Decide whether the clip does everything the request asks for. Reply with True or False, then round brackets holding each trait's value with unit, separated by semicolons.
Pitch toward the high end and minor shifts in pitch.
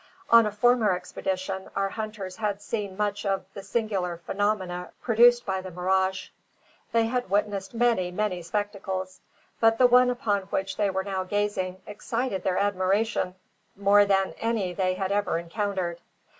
True (200 Hz; 2.3 semitones)